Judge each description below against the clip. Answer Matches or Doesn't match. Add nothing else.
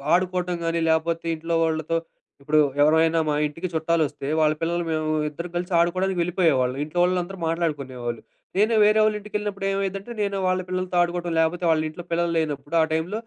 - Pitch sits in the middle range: Matches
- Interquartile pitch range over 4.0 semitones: Doesn't match